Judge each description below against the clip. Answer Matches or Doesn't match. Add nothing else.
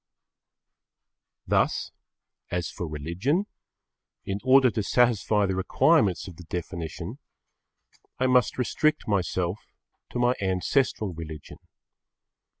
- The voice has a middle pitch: Doesn't match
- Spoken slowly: Matches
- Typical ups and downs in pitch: Doesn't match